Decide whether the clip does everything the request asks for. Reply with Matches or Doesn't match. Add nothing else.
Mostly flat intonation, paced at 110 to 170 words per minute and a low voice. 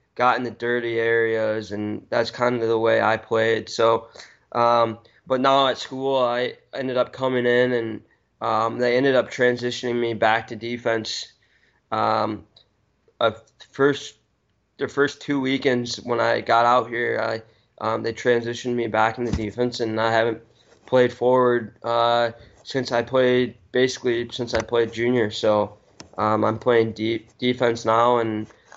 Matches